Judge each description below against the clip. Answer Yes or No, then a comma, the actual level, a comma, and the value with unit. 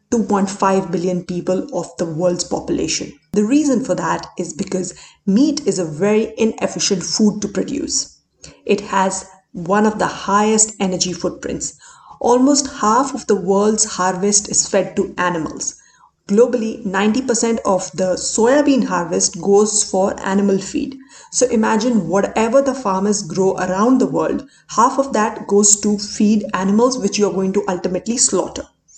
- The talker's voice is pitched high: Yes, high, 205 Hz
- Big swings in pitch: No, average, 3.3 semitones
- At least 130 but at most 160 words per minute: Yes, average, 150 wpm